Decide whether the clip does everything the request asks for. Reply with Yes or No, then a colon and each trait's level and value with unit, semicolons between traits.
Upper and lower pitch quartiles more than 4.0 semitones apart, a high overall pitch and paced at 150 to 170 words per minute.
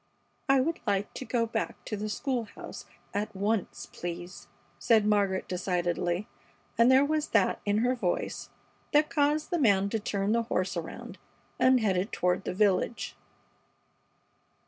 Yes: average, 4.6 semitones; high, 210 Hz; average, 155 wpm